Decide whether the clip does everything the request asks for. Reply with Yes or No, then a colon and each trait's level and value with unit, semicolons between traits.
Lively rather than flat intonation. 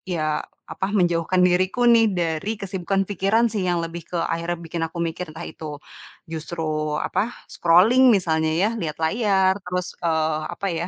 No: average, 3.2 semitones